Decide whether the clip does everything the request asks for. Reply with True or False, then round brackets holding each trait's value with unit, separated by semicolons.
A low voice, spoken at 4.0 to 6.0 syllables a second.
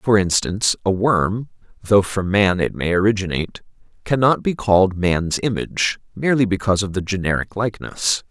True (100 Hz; 5.4 syllables/s)